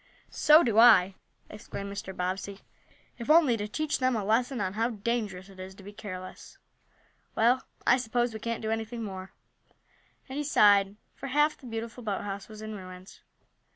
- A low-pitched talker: No, high, 215 Hz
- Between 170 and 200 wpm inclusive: Yes, average, 175 wpm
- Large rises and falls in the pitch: No, average, 3.6 semitones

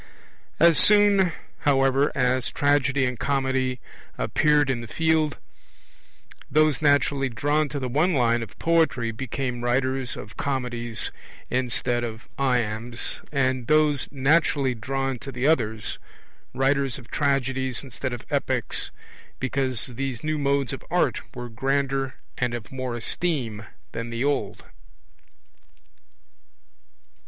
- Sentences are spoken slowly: Yes, slow, 120 wpm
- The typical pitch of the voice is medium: No, low, 130 Hz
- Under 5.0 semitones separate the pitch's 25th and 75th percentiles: Yes, average, 2.7 semitones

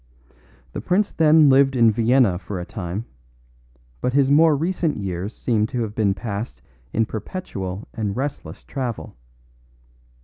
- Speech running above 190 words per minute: No, average, 140 wpm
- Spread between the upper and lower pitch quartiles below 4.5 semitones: No, wide, 5.6 semitones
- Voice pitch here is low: Yes, low, 115 Hz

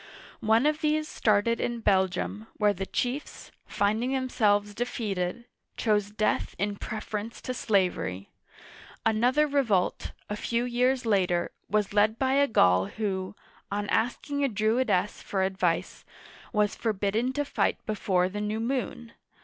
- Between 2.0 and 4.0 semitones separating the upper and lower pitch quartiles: Yes, average, 3.4 semitones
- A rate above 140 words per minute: No, slow, 135 wpm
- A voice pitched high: Yes, high, 215 Hz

